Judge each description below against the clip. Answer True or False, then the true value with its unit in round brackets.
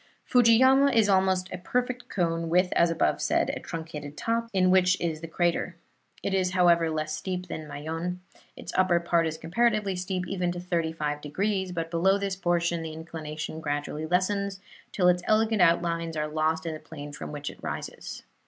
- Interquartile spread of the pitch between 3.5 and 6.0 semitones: False (2.8 semitones)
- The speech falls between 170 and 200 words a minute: True (185 wpm)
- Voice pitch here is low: False (175 Hz)